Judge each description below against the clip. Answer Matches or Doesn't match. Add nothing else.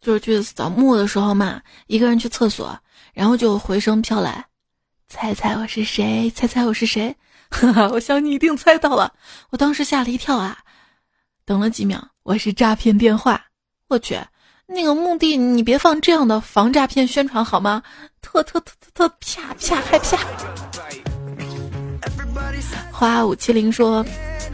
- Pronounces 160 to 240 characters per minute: Matches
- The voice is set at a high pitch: Matches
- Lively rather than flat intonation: Doesn't match